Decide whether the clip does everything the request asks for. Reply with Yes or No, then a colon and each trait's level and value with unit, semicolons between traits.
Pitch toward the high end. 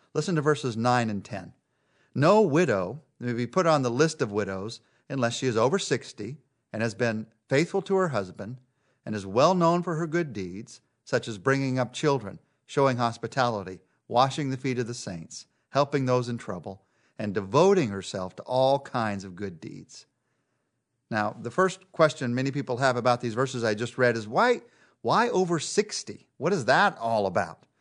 No: low, 125 Hz